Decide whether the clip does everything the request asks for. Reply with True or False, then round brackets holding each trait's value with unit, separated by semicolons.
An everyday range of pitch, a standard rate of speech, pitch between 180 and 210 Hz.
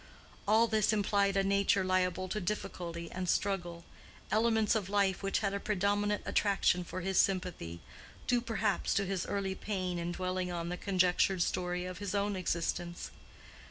False (2.2 semitones; 160 wpm; 190 Hz)